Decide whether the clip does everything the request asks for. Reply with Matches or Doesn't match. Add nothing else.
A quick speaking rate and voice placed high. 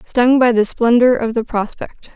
Doesn't match